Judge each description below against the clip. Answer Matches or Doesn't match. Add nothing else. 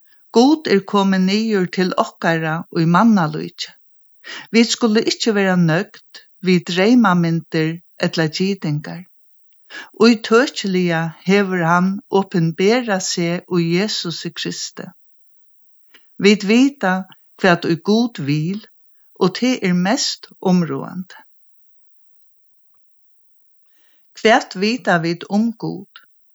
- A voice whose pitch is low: Doesn't match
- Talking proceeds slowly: Matches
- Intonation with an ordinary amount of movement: Matches